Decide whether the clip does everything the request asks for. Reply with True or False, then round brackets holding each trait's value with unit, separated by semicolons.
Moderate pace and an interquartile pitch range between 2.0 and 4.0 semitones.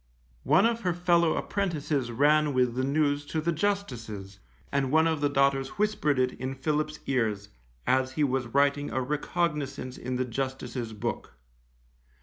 True (155 wpm; 3.3 semitones)